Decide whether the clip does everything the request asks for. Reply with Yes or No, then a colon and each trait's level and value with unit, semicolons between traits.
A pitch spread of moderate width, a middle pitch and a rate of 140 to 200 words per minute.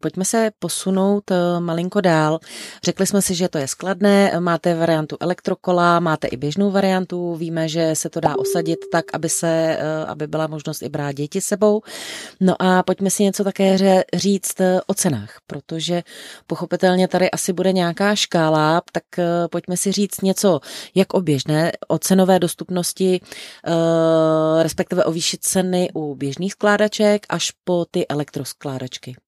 Yes: average, 3.0 semitones; medium, 175 Hz; average, 150 wpm